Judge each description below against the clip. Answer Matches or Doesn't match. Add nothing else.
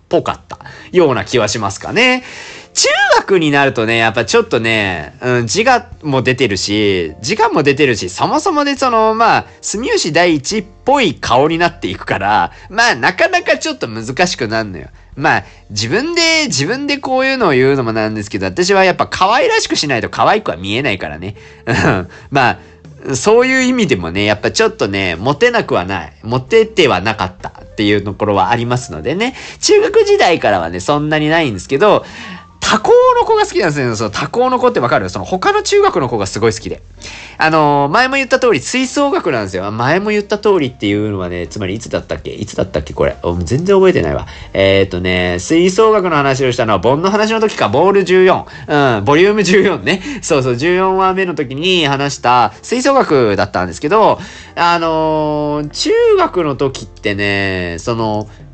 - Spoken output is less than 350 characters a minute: Doesn't match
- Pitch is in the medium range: Matches